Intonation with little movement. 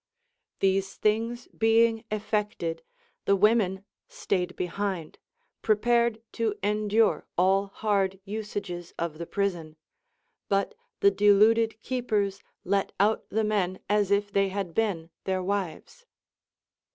Yes: narrow, 2.3 semitones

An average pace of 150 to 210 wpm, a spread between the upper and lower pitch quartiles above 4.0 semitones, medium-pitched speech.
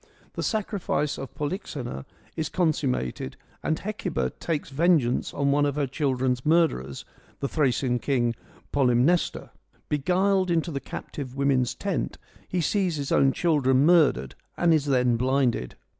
No: slow, 135 wpm; average, 4.7 semitones; medium, 145 Hz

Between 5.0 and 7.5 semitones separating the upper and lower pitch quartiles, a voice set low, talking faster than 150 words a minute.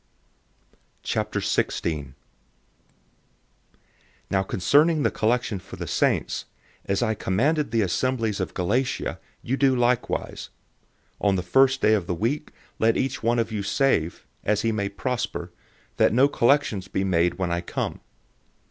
No: average, 5.3 semitones; low, 110 Hz; average, 140 wpm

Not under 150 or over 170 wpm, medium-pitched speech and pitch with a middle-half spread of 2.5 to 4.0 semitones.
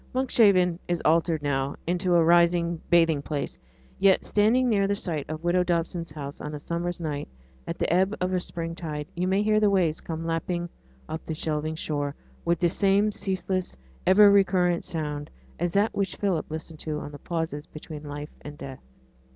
No: average, 185 wpm; medium, 170 Hz; average, 3.3 semitones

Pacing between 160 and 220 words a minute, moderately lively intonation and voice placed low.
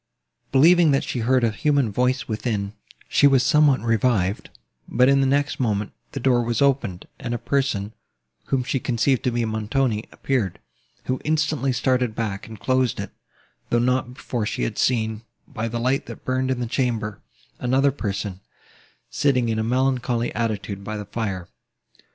Yes: average, 170 wpm; average, 3.3 semitones; low, 120 Hz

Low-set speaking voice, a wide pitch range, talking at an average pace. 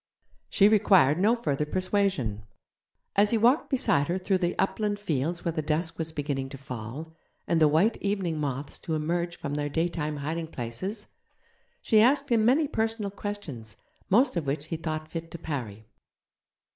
No: medium, 165 Hz; wide, 5.8 semitones; average, 170 wpm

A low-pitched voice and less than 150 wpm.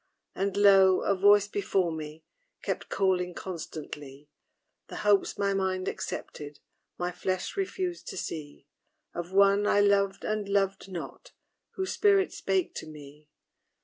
No: high, 190 Hz; slow, 135 wpm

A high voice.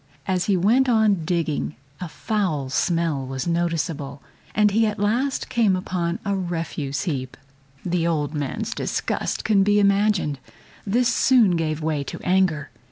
No: medium, 175 Hz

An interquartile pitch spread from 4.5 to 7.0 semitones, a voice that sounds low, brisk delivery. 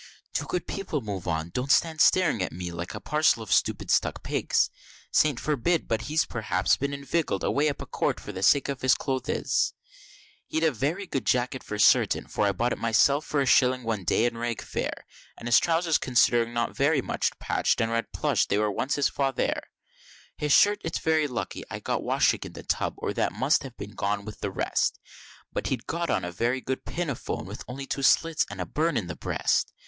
Yes: wide, 5.4 semitones; low, 130 Hz; fast, 215 wpm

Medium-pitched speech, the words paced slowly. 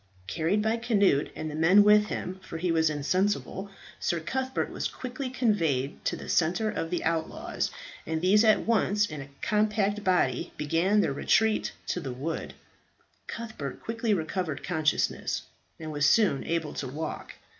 No: medium, 180 Hz; average, 160 wpm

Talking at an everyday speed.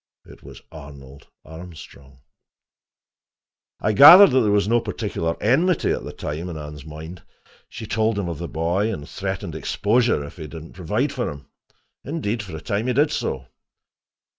Yes: average, 170 wpm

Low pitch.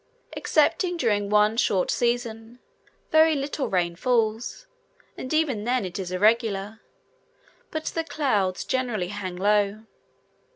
No: high, 220 Hz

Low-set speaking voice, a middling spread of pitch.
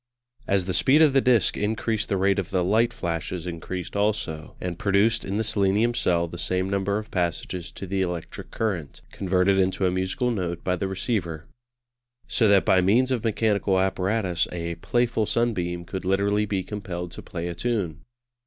Yes: very low, 95 Hz; average, 3.3 semitones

